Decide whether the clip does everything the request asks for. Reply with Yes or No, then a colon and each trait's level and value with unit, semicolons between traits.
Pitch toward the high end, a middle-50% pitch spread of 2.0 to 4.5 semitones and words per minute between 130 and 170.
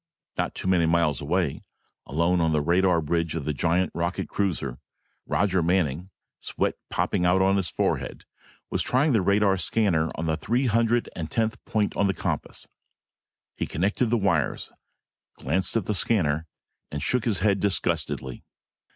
No: very low, 90 Hz; average, 3.9 semitones; average, 160 wpm